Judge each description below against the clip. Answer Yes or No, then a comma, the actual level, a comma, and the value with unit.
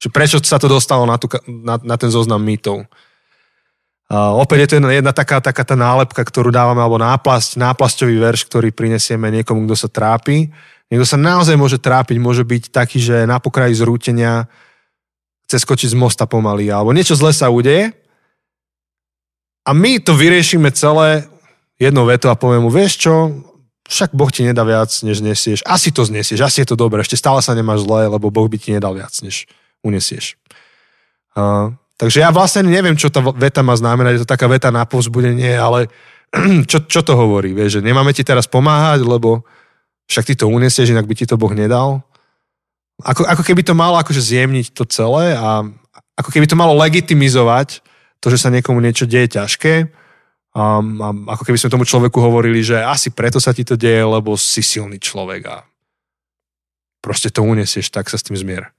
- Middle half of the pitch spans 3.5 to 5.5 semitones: Yes, average, 3.8 semitones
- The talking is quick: Yes, fast, 185 wpm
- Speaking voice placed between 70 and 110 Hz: No, low, 125 Hz